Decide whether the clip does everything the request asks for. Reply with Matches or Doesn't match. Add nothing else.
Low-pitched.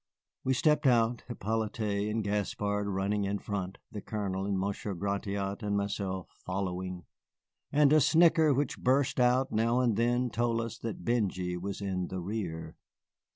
Matches